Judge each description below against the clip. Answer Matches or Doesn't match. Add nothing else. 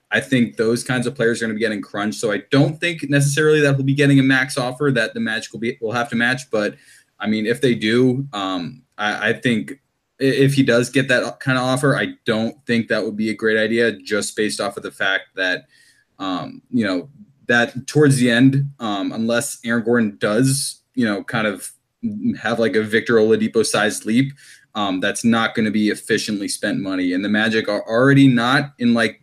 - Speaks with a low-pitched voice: Matches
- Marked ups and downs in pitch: Doesn't match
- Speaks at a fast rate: Matches